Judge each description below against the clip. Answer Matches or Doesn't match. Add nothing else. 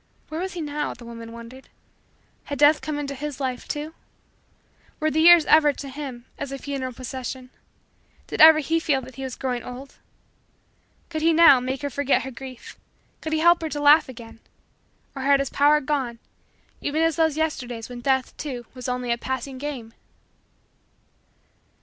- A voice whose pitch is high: Matches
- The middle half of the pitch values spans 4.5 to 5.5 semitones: Doesn't match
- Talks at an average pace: Matches